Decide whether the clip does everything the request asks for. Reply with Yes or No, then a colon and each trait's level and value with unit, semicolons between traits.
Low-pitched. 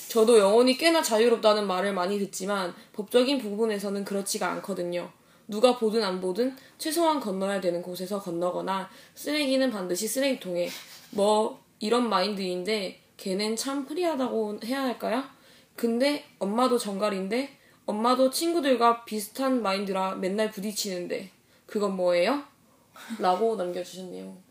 No: high, 215 Hz